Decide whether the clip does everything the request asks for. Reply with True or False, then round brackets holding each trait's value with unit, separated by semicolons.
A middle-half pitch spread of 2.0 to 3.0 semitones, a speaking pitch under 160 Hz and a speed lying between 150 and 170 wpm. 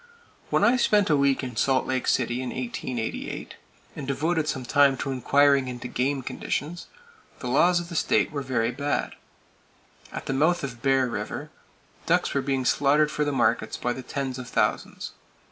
False (2.4 semitones; 135 Hz; 180 wpm)